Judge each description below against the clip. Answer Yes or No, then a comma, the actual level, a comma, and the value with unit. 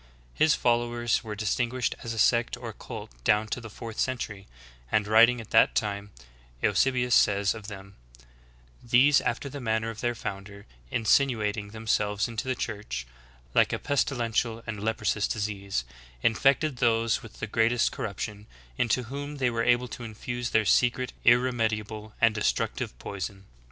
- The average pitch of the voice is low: Yes, low, 115 Hz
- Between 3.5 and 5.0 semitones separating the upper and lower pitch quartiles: No, average, 2.7 semitones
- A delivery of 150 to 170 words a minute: Yes, average, 155 wpm